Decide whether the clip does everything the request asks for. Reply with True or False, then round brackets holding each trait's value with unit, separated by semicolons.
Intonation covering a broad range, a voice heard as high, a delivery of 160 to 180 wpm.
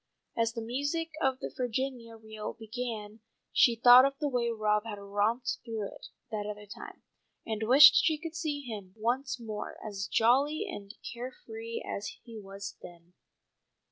False (3.5 semitones; 230 Hz; 165 wpm)